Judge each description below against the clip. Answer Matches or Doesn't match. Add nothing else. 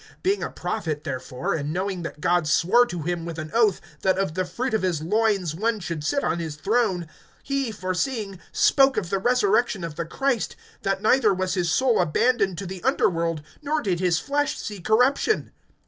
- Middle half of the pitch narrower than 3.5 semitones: Doesn't match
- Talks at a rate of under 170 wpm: Doesn't match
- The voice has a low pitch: Doesn't match